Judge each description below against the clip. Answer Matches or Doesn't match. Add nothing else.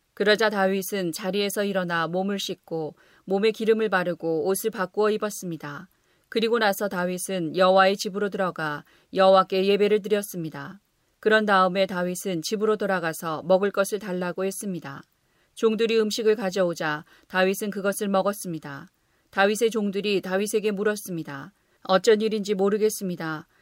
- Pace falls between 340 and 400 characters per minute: Matches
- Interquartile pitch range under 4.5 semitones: Matches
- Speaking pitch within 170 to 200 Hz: Matches